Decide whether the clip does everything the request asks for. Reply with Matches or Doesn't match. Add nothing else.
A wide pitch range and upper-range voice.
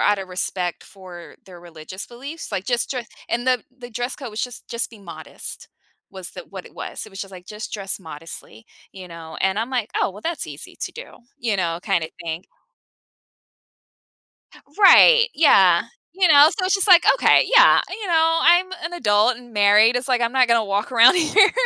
Matches